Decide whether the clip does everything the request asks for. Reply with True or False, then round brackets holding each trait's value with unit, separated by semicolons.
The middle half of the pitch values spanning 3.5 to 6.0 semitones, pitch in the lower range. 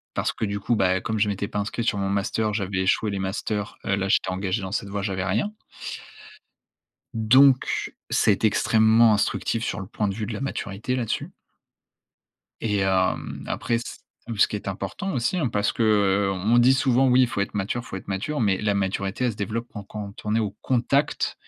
False (2.9 semitones; 105 Hz)